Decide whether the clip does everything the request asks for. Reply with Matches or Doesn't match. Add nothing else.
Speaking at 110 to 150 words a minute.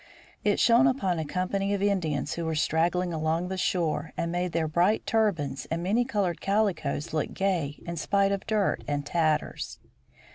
Doesn't match